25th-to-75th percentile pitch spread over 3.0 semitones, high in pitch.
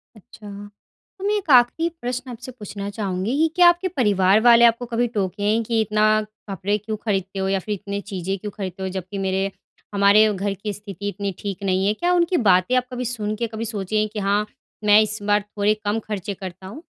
No: average, 2.7 semitones; high, 210 Hz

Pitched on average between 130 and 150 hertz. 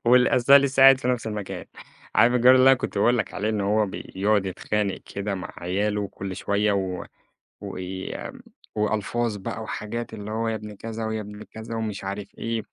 No: low, 105 Hz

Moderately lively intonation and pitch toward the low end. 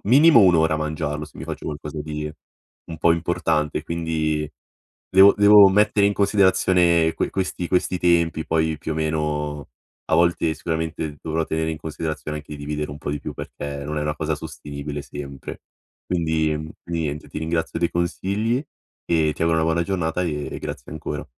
No: narrow, 2.2 semitones; very low, 80 Hz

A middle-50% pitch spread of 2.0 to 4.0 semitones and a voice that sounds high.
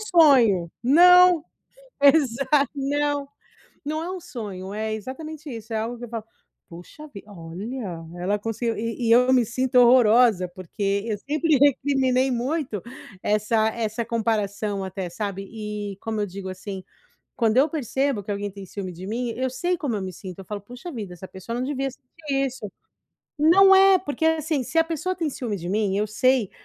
No: wide, 5.5 semitones; high, 235 Hz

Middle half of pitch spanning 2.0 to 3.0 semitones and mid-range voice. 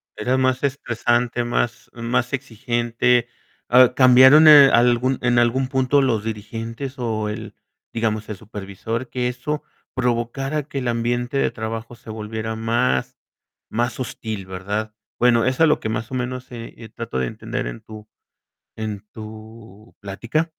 No: narrow, 2.6 semitones; low, 120 Hz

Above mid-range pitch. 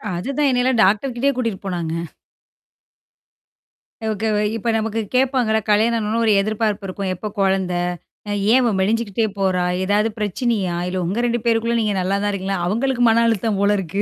Yes: high, 215 Hz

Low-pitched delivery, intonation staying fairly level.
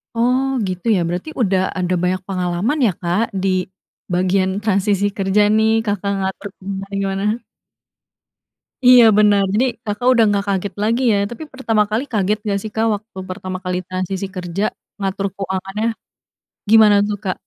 No: high, 200 Hz; narrow, 2.3 semitones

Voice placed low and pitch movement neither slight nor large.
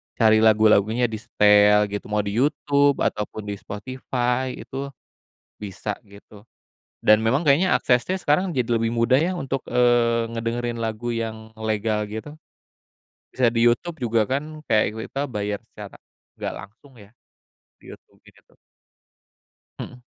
Yes: low, 115 Hz; average, 3.3 semitones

